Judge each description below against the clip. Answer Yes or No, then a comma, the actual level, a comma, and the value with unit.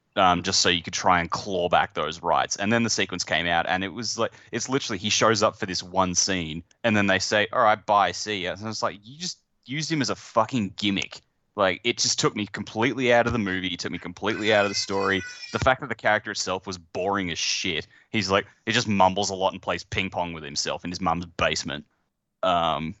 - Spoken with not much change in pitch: No, average, 3.6 semitones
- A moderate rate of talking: No, fast, 250 wpm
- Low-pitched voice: Yes, low, 105 Hz